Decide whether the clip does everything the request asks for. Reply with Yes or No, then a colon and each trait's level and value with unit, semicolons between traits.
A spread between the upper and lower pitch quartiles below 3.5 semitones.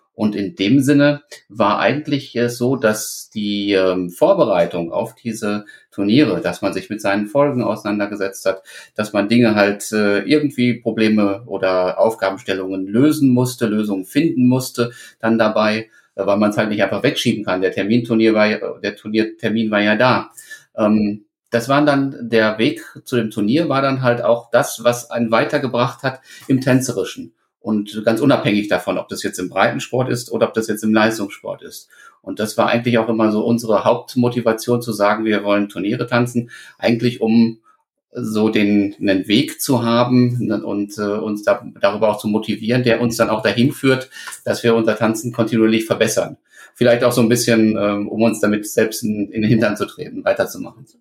Yes: narrow, 2.6 semitones